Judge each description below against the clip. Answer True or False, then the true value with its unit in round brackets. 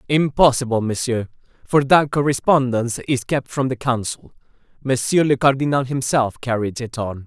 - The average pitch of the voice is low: True (130 Hz)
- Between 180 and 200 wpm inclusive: False (140 wpm)